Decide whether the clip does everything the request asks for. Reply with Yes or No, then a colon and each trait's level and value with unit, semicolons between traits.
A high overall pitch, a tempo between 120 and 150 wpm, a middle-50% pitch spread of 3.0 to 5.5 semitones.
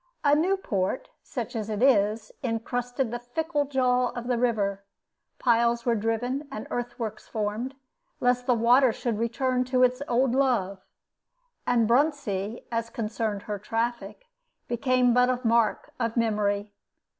No: high, 235 Hz; average, 145 wpm; narrow, 2.4 semitones